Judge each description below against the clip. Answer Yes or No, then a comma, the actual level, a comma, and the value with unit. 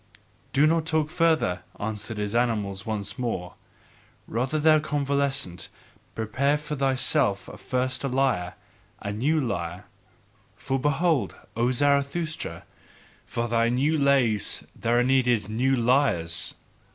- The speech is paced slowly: Yes, slow, 120 wpm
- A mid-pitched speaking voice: No, low, 130 Hz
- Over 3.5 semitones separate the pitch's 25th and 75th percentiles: Yes, average, 4.6 semitones